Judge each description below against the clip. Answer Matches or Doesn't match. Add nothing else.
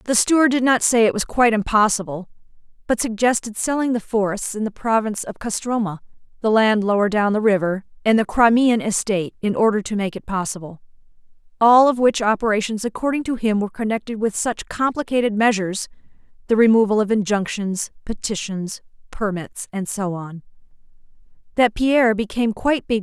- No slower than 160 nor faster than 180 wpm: Matches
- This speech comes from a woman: Matches